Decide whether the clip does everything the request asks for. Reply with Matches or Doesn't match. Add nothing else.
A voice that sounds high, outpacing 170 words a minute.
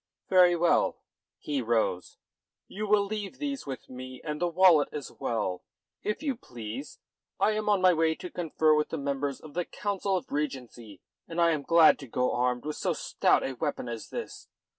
Doesn't match